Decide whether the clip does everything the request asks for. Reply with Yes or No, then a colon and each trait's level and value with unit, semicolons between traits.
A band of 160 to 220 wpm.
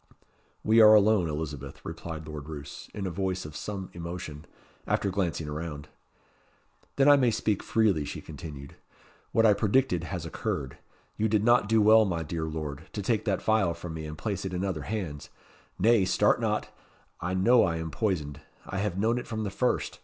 Yes: average, 190 wpm